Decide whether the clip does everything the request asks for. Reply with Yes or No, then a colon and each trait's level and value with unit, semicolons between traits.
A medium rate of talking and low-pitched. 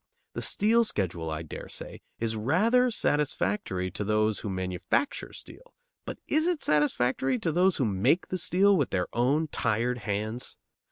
Yes: average, 160 wpm; low, 125 Hz